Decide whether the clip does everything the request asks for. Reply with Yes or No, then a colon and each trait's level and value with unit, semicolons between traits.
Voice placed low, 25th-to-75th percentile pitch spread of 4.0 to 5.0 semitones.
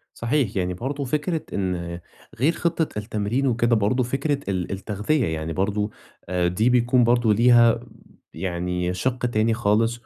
Yes: low, 115 Hz; average, 4.6 semitones